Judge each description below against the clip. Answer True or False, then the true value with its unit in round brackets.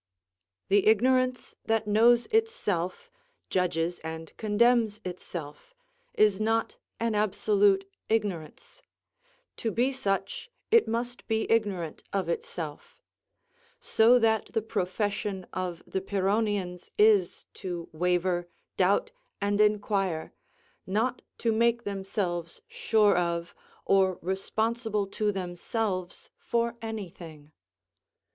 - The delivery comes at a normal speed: False (105 wpm)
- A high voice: True (205 Hz)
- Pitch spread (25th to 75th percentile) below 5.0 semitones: True (3.7 semitones)